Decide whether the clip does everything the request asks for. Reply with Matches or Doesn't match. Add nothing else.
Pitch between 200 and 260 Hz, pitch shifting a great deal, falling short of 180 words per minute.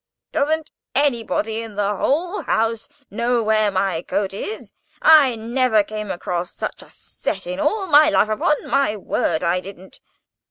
Matches